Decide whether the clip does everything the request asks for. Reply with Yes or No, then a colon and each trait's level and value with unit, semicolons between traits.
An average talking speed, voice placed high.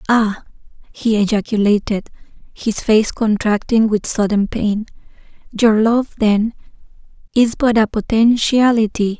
No: slow, 105 wpm; high, 220 Hz